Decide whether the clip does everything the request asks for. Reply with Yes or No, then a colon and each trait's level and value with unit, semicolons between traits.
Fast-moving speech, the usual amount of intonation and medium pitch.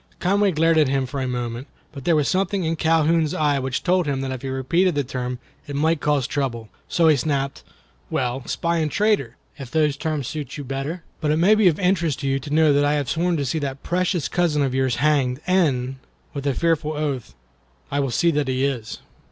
Yes: fast, 220 wpm; average, 3.7 semitones; medium, 145 Hz